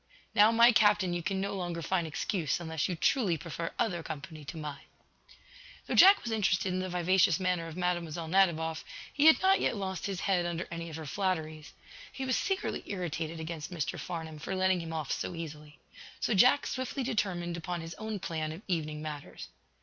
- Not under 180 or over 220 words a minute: Yes, average, 195 wpm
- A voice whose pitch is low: No, medium, 175 Hz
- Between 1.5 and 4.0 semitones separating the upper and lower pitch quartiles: Yes, average, 3.3 semitones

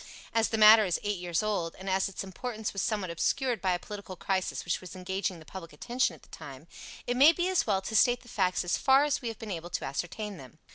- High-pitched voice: Yes, high, 195 Hz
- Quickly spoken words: Yes, fast, 255 wpm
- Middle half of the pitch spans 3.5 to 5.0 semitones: Yes, average, 4.1 semitones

